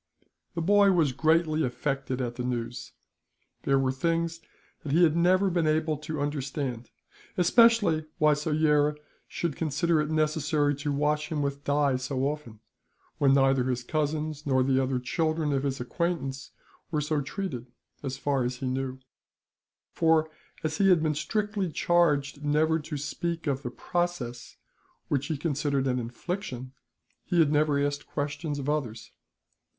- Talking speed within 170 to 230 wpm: No, average, 155 wpm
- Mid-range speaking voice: Yes, medium, 150 Hz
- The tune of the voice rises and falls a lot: No, average, 3.0 semitones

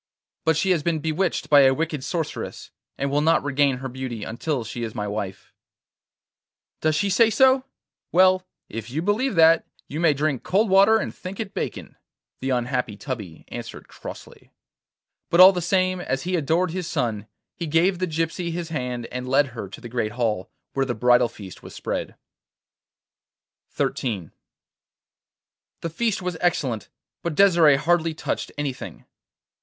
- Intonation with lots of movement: Yes, wide, 6.1 semitones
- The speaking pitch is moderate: Yes, medium, 155 Hz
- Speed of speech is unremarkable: Yes, average, 165 wpm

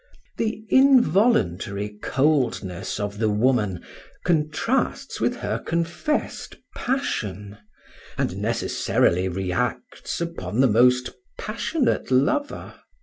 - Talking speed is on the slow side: Yes, slow, 85 wpm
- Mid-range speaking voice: No, low, 125 Hz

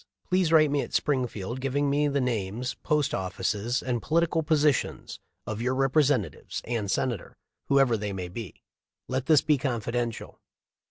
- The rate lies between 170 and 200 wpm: No, average, 155 wpm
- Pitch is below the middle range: Yes, low, 130 Hz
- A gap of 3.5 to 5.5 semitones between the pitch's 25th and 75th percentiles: Yes, average, 4.4 semitones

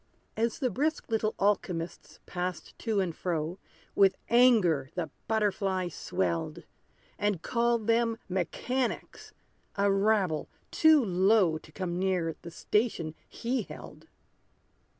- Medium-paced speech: No, slow, 115 wpm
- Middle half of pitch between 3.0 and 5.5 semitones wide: Yes, average, 4.6 semitones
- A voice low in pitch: No, high, 195 Hz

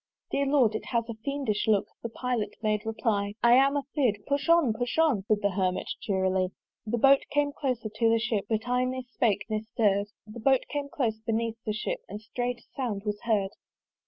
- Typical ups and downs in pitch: Yes, average, 3.4 semitones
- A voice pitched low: No, high, 230 Hz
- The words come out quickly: Yes, fast, 210 wpm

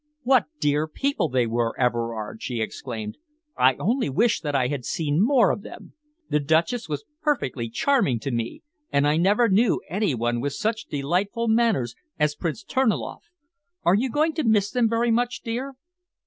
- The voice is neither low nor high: Yes, medium, 170 Hz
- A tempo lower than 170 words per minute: No, average, 175 wpm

